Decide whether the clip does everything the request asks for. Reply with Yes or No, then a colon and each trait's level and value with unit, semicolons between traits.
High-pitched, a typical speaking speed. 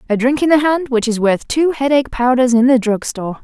No: very high, 255 Hz; fast, 245 wpm